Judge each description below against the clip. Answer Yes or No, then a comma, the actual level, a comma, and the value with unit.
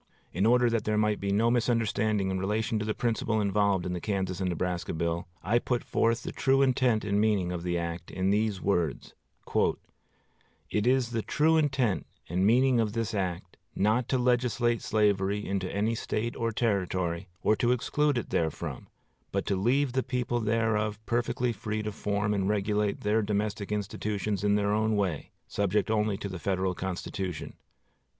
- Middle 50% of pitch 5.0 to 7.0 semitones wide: No, average, 3.1 semitones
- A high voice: No, low, 105 Hz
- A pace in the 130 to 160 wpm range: No, average, 175 wpm